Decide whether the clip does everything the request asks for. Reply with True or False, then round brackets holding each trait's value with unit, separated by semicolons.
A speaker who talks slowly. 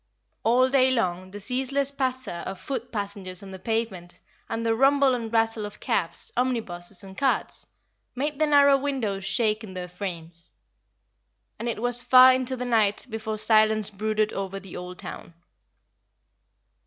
False (155 wpm)